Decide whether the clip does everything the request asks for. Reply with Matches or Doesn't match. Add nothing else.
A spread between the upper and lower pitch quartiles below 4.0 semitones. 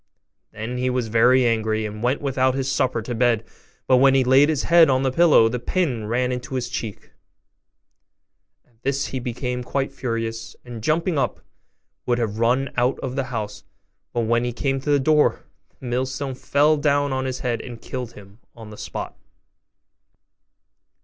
Matches